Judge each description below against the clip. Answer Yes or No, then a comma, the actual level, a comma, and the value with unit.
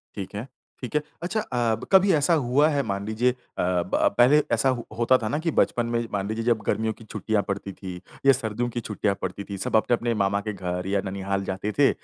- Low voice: Yes, low, 110 Hz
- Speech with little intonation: No, average, 3.9 semitones